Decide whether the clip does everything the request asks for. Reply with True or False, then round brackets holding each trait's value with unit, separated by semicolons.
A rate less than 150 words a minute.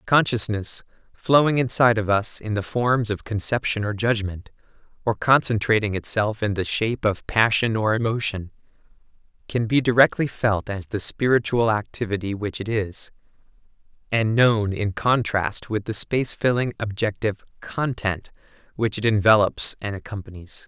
True (140 wpm)